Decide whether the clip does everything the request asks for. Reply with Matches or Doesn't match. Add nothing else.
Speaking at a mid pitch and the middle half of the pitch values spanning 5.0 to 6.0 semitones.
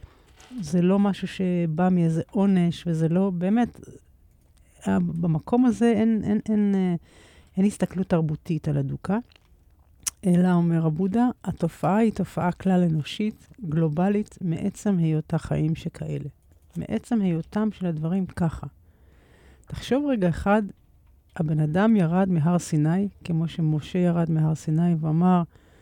Doesn't match